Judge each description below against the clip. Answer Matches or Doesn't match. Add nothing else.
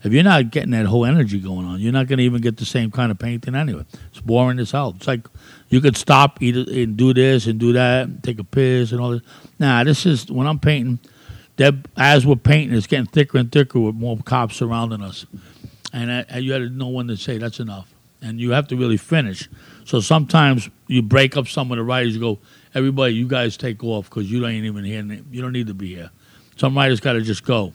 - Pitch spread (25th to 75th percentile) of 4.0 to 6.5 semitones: Doesn't match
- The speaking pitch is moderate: Doesn't match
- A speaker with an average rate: Doesn't match